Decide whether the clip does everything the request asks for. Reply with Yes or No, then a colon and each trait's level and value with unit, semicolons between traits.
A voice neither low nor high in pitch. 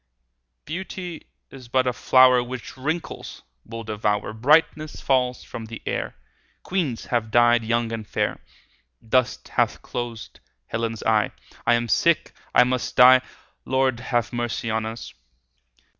No: low, 120 Hz